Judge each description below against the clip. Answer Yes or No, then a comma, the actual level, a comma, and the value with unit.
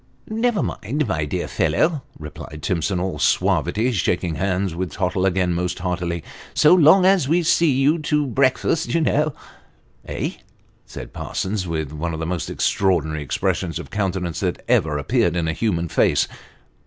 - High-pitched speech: No, very low, 95 Hz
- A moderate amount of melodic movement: No, wide, 8.9 semitones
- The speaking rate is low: No, average, 170 wpm